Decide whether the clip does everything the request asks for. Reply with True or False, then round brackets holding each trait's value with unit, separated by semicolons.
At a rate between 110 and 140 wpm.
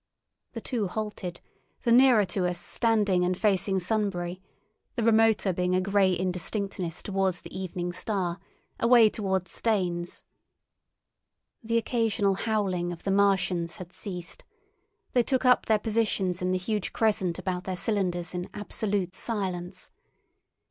True (135 wpm)